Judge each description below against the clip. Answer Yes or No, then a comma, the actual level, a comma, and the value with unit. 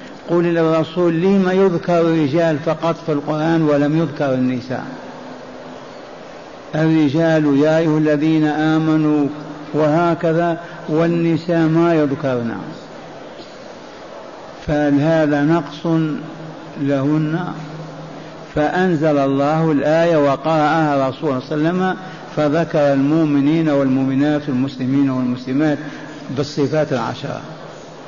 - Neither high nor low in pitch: Yes, medium, 155 Hz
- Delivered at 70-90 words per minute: Yes, average, 85 wpm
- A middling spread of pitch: No, narrow, 2.2 semitones